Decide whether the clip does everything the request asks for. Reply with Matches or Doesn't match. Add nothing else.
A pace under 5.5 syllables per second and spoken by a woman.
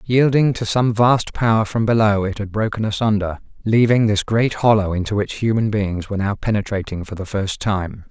Doesn't match